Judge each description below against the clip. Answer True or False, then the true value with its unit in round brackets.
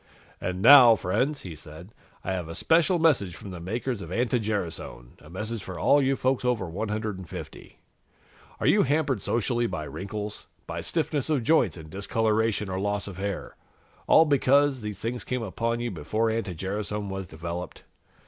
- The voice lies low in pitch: True (105 Hz)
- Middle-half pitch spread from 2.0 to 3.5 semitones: False (4.9 semitones)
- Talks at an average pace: True (170 wpm)